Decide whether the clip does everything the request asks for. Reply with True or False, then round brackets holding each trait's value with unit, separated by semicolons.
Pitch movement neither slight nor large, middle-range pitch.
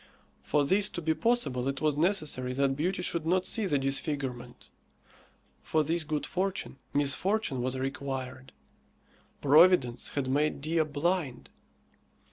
True (4.5 semitones; 145 Hz)